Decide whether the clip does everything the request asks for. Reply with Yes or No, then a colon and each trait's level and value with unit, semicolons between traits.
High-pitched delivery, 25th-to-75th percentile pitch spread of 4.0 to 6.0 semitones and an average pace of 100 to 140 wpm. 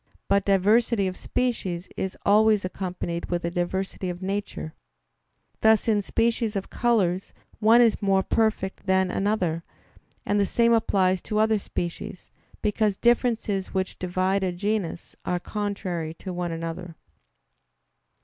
No: high, 195 Hz; average, 3.0 semitones; slow, 135 wpm